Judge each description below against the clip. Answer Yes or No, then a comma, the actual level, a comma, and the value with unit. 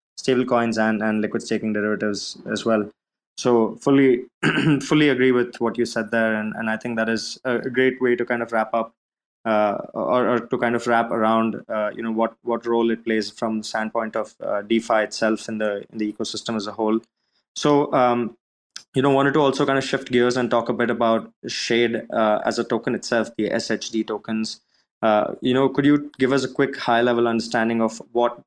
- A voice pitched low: Yes, low, 115 Hz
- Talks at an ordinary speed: No, fast, 215 wpm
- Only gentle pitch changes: Yes, narrow, 2.0 semitones